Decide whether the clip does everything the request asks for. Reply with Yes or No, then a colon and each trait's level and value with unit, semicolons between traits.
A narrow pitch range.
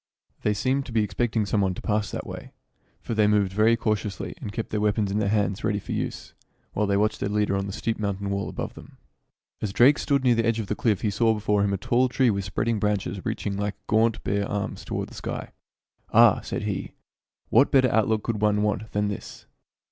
Yes: narrow, 1.9 semitones